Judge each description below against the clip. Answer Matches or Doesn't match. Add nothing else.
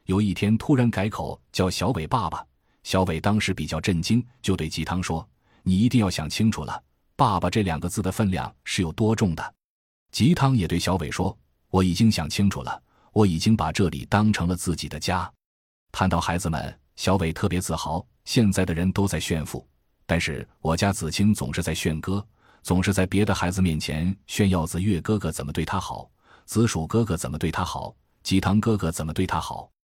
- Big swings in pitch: Doesn't match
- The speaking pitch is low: Matches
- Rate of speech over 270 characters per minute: Matches